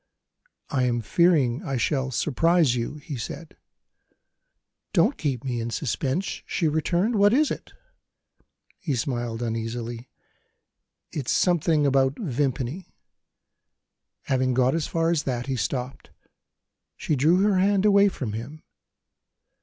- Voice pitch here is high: No, medium, 140 Hz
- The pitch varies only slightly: No, wide, 5.5 semitones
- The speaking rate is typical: No, slow, 125 wpm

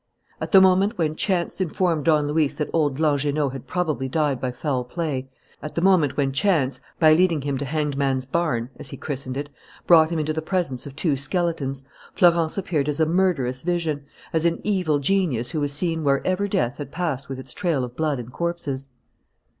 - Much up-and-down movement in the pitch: No, average, 3.9 semitones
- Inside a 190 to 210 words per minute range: Yes, average, 200 wpm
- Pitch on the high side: No, medium, 150 Hz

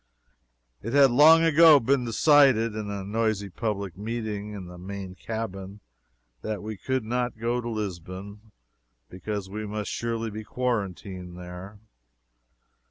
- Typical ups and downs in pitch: Yes, average, 3.2 semitones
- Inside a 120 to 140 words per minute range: Yes, slow, 135 wpm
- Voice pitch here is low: Yes, low, 110 Hz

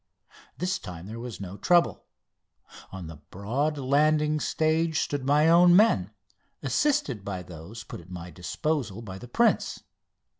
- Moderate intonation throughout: No, wide, 8.7 semitones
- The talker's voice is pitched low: Yes, low, 125 Hz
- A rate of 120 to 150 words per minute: Yes, average, 145 wpm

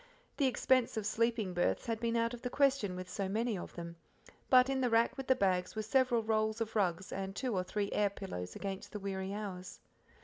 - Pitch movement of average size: Yes, average, 3.7 semitones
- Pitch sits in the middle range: No, high, 215 Hz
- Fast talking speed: Yes, fast, 225 wpm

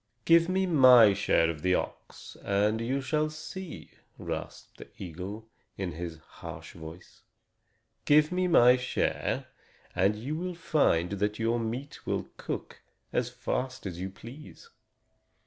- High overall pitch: No, low, 115 Hz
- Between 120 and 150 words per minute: Yes, average, 140 wpm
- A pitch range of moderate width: No, wide, 8.1 semitones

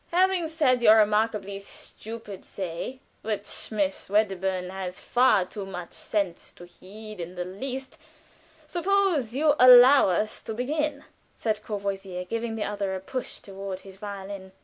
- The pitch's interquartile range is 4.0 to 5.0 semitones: Yes, average, 4.6 semitones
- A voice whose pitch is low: No, high, 210 Hz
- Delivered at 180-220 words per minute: No, average, 145 wpm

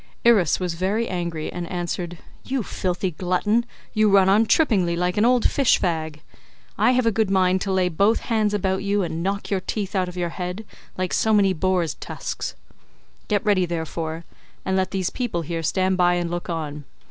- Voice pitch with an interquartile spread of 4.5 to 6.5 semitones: No, average, 2.9 semitones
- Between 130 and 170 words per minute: No, average, 195 wpm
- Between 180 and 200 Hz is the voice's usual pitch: Yes, medium, 185 Hz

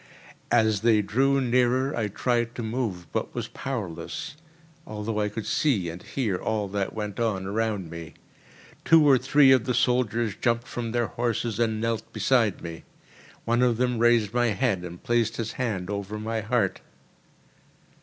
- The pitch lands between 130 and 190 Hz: No, low, 115 Hz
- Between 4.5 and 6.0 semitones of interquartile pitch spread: No, average, 2.8 semitones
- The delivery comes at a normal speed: Yes, average, 165 wpm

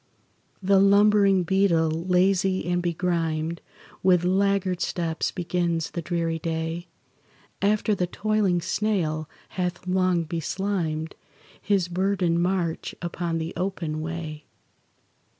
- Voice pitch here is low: No, medium, 175 Hz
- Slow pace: Yes, slow, 105 wpm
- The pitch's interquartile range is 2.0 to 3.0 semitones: Yes, narrow, 2.6 semitones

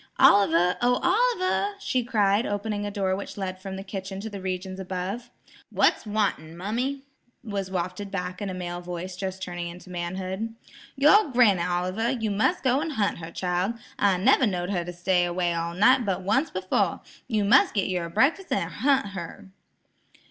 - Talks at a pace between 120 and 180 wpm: Yes, average, 175 wpm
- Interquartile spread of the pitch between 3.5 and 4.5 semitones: Yes, average, 3.8 semitones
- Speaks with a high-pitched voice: Yes, high, 195 Hz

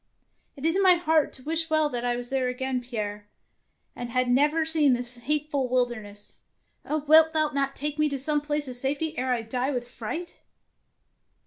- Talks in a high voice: Yes, very high, 275 Hz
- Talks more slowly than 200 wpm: No, fast, 205 wpm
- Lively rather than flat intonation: No, average, 3.8 semitones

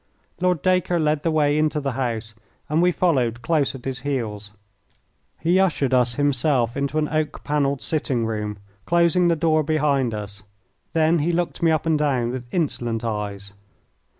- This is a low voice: No, medium, 145 Hz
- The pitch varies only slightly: No, average, 5.0 semitones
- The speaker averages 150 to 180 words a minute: Yes, average, 170 wpm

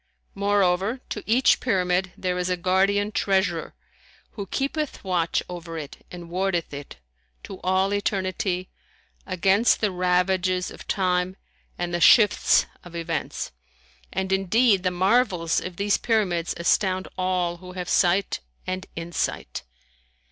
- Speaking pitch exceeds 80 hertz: Yes, medium, 185 Hz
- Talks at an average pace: No, slow, 130 wpm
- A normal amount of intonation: No, narrow, 1.8 semitones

